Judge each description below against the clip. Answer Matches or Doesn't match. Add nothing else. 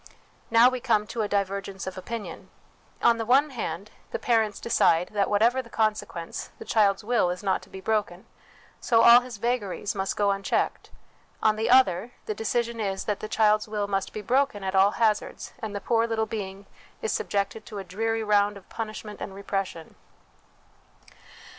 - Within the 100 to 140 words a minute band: Doesn't match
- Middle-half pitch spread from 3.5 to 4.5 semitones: Doesn't match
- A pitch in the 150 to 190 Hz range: Doesn't match